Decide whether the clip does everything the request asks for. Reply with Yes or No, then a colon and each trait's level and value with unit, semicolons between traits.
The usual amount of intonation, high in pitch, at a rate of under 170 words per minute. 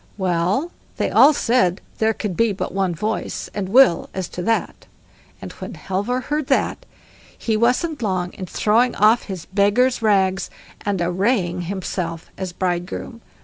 Yes: average, 4.1 semitones; high, 200 Hz; average, 150 wpm